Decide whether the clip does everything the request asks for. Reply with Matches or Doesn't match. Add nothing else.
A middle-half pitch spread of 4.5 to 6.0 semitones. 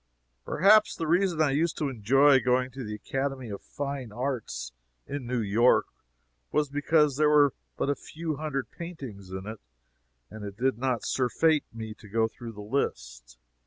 Matches